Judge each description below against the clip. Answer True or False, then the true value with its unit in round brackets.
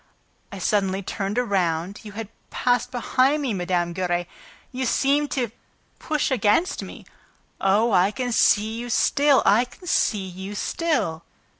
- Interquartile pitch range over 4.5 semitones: True (4.9 semitones)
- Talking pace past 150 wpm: False (145 wpm)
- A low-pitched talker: False (215 Hz)